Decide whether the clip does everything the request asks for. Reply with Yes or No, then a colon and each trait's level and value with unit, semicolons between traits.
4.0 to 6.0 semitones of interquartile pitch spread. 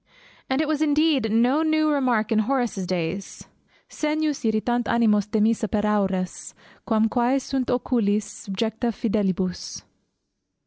Yes: average, 4.3 semitones